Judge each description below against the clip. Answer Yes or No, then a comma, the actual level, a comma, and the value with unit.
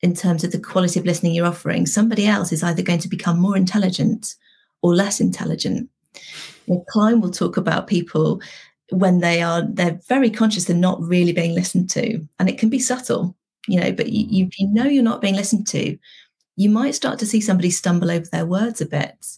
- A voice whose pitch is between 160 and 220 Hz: Yes, medium, 185 Hz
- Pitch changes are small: No, average, 3.8 semitones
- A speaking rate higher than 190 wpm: Yes, fast, 205 wpm